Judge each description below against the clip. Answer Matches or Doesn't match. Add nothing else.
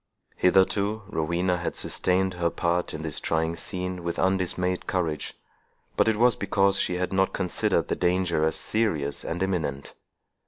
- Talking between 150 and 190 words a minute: Matches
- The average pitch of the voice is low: Matches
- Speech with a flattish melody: Matches